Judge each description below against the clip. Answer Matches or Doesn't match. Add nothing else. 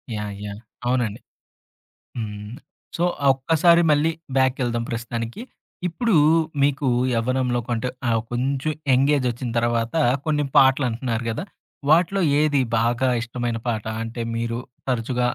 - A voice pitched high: Doesn't match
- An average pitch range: Matches